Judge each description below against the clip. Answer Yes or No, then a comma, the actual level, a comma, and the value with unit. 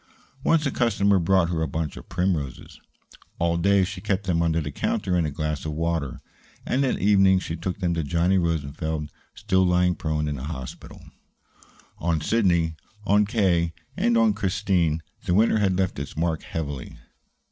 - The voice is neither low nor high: No, very low, 85 Hz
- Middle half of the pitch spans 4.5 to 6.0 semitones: No, average, 3.3 semitones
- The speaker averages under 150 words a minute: No, average, 175 wpm